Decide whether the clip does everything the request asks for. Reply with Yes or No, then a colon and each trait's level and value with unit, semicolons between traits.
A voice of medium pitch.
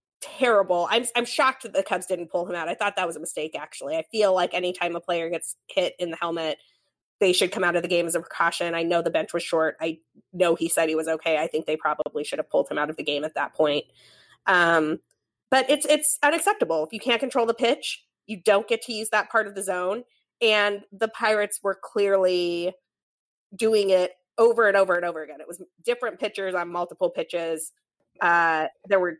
Yes: medium, 180 Hz